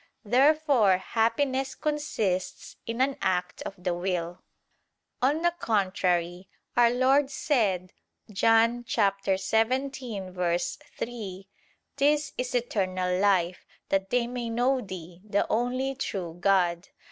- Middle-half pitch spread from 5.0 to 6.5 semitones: Yes, wide, 5.5 semitones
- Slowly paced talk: Yes, slow, 105 wpm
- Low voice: No, high, 215 Hz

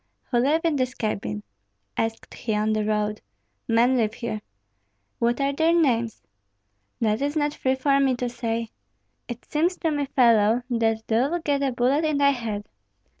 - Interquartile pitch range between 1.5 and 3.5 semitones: No, average, 4.0 semitones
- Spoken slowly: No, average, 175 wpm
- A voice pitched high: Yes, high, 245 Hz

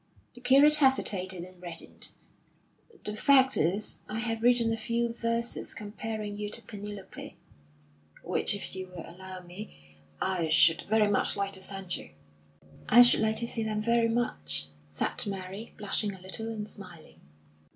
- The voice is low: No, high, 210 Hz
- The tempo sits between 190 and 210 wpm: No, average, 160 wpm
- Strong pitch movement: No, average, 3.7 semitones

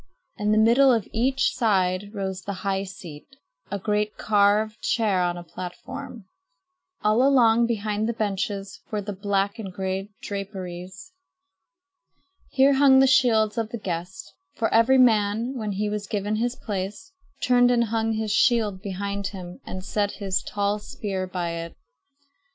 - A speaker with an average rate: Yes, average, 155 wpm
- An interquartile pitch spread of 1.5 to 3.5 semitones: Yes, average, 2.9 semitones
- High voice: Yes, high, 210 Hz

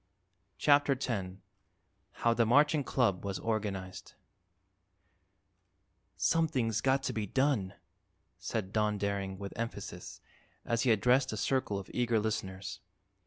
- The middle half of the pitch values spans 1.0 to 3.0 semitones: No, average, 4.7 semitones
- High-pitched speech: No, low, 110 Hz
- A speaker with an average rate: No, slow, 120 wpm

